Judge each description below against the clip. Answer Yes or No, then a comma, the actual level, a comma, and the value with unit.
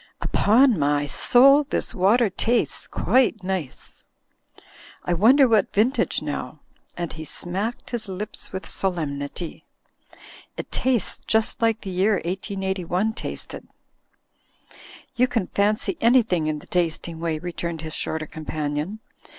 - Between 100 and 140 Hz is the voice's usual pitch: No, high, 190 Hz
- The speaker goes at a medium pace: No, slow, 125 wpm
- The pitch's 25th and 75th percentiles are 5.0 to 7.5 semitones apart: Yes, wide, 5.4 semitones